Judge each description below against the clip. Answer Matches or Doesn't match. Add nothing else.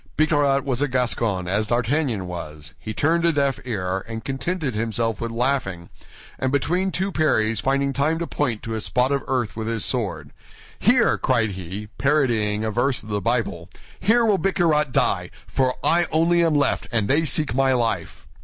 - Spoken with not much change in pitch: Doesn't match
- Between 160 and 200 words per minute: Matches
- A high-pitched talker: Doesn't match